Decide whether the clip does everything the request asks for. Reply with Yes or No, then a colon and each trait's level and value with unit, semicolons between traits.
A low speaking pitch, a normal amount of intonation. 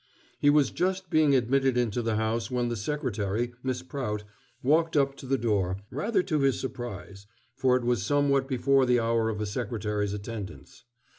Yes: low, 125 Hz; average, 3.9 semitones